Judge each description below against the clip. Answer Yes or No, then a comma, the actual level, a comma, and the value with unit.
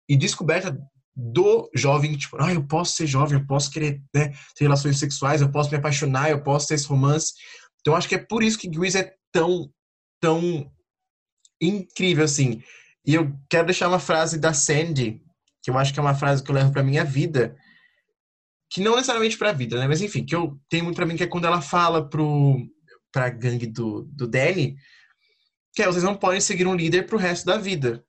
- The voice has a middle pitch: Yes, medium, 155 Hz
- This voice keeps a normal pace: No, fast, 210 wpm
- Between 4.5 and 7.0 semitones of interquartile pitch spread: No, average, 4.1 semitones